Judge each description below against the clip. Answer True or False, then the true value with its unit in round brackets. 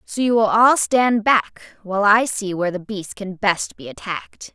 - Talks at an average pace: False (210 wpm)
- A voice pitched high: True (205 Hz)